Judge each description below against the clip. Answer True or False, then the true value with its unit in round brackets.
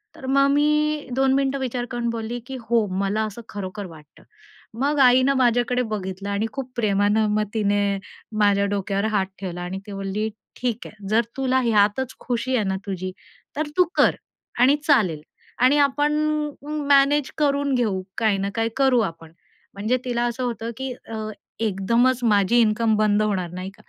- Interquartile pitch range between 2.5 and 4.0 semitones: False (4.4 semitones)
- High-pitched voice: True (225 Hz)